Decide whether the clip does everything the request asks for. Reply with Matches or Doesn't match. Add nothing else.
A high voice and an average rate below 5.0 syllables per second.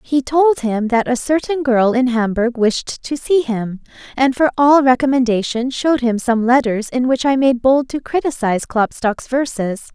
Matches